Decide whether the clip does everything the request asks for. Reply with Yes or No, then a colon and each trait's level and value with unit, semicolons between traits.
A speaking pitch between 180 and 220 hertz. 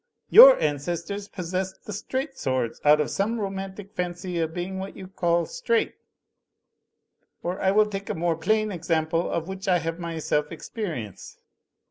Yes: medium, 185 Hz